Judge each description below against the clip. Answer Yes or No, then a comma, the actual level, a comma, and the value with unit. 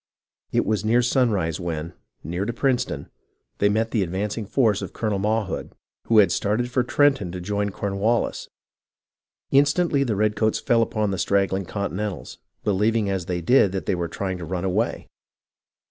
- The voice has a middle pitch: No, low, 105 Hz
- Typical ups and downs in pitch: Yes, average, 3.2 semitones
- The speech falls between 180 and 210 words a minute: No, average, 160 wpm